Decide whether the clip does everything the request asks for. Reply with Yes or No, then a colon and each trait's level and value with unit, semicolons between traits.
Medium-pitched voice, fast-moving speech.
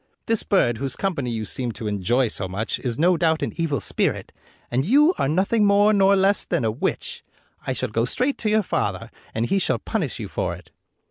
Yes: medium, 160 Hz; fast, 215 wpm